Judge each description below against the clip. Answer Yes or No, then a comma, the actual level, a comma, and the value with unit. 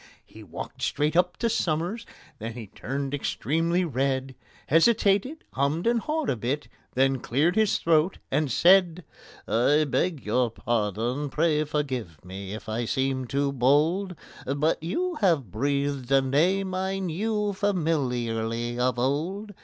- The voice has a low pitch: No, medium, 145 Hz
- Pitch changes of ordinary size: No, wide, 6.1 semitones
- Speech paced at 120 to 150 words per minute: Yes, average, 140 wpm